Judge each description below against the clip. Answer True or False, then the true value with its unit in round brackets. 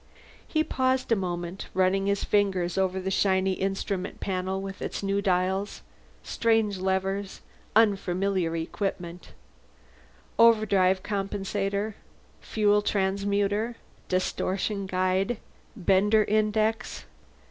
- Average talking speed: False (95 wpm)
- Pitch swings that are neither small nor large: False (1.8 semitones)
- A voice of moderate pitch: False (195 Hz)